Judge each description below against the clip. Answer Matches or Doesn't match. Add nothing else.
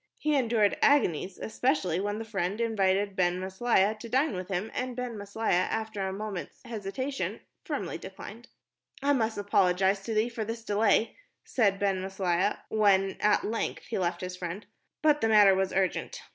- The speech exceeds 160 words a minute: Matches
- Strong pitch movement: Doesn't match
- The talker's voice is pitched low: Doesn't match